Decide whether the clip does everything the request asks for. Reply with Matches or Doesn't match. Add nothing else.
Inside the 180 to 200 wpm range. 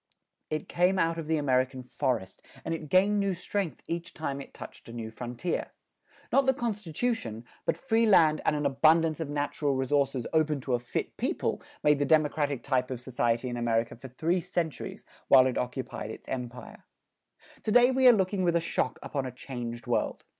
Matches